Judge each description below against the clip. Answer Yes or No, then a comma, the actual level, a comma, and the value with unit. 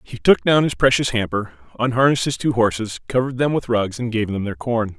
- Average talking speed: No, fast, 230 wpm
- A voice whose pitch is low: Yes, low, 115 Hz